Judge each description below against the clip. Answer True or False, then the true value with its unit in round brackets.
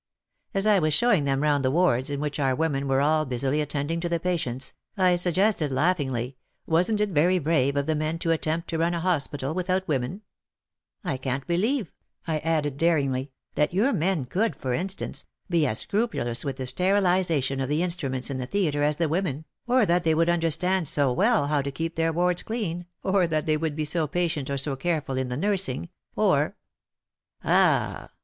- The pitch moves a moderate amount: True (4.3 semitones)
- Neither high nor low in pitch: True (160 Hz)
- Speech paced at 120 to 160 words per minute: False (200 wpm)